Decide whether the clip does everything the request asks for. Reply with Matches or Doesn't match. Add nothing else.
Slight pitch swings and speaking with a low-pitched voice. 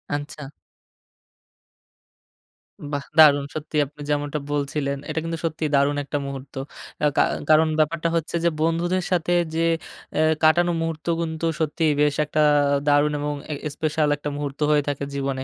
Doesn't match